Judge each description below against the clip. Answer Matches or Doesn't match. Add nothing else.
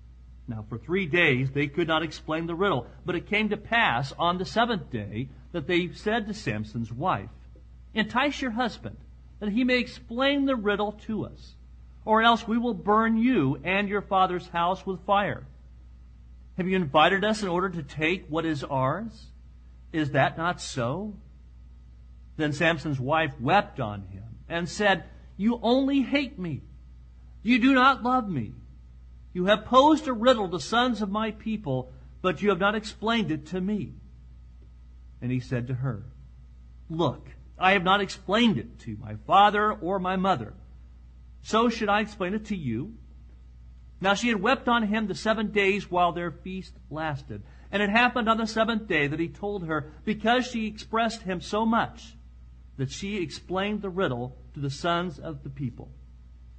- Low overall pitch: Doesn't match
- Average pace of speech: Matches